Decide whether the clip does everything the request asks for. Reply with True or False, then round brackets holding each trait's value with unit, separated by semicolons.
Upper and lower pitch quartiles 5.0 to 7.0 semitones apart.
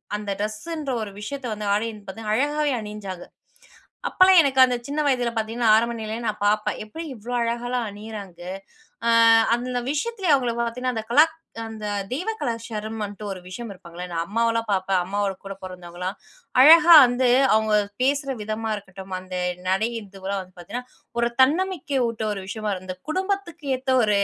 False (4.2 semitones)